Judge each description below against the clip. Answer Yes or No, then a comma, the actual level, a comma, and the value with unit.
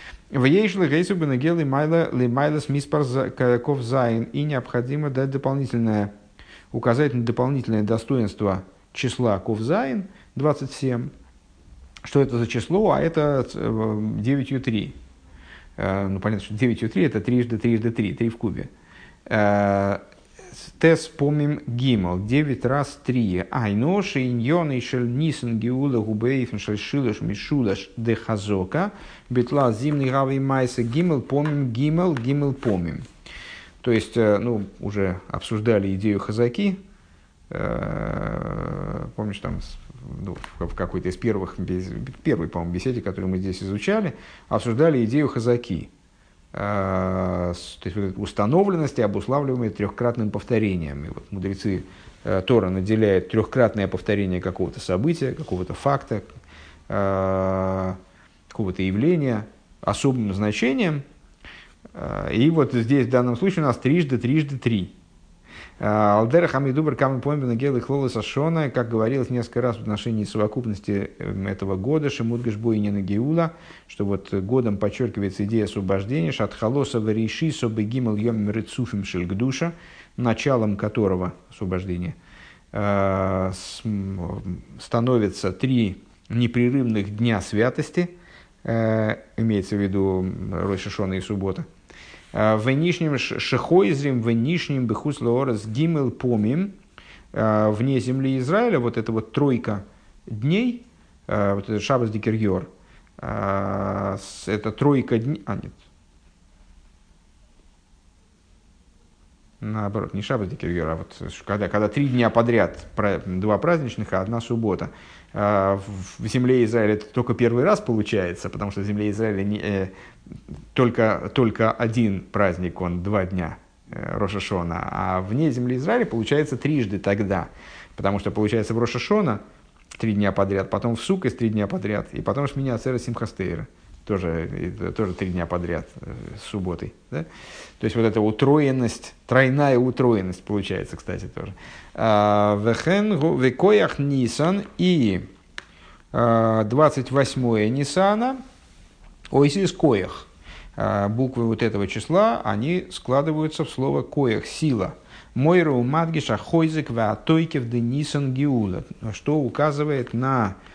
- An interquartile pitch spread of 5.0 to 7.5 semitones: Yes, wide, 5.5 semitones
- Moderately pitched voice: No, low, 115 Hz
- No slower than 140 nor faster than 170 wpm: No, slow, 110 wpm